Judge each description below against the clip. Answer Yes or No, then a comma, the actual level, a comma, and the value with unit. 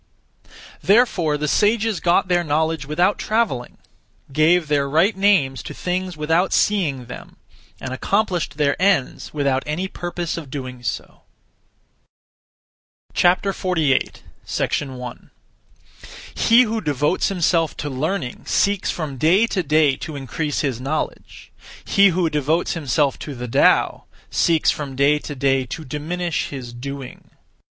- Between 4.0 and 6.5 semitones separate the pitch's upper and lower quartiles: Yes, average, 4.5 semitones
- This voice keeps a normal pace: No, slow, 130 wpm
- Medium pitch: Yes, medium, 155 Hz